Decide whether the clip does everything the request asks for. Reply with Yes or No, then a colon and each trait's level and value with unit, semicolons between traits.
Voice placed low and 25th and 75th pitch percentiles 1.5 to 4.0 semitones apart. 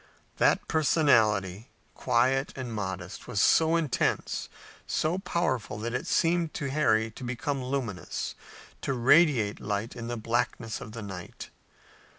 No: low, 120 Hz; average, 4.8 semitones